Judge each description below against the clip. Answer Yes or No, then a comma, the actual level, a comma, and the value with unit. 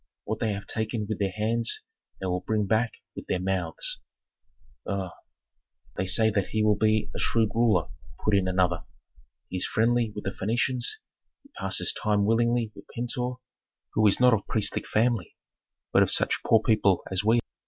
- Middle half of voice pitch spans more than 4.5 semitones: No, average, 2.9 semitones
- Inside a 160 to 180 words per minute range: Yes, average, 175 wpm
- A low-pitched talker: Yes, low, 110 Hz